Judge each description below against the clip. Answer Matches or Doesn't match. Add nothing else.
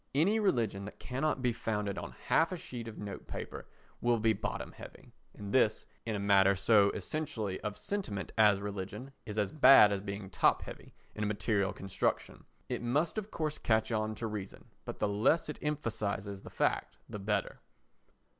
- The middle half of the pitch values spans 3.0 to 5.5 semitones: Matches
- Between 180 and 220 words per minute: Matches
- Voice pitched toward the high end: Doesn't match